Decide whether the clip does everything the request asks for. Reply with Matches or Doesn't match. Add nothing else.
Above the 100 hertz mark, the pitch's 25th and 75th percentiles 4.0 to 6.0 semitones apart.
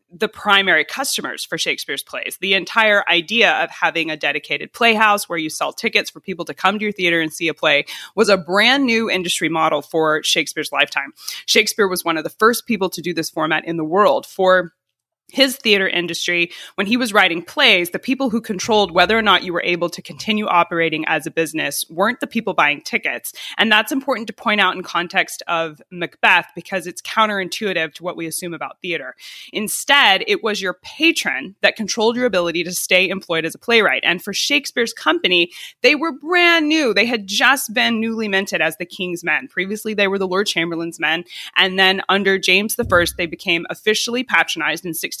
Matches